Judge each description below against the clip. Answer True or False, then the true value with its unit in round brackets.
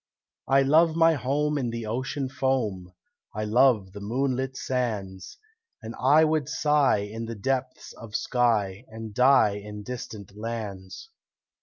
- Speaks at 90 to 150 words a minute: True (140 wpm)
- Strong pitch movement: False (4.3 semitones)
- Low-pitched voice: True (120 Hz)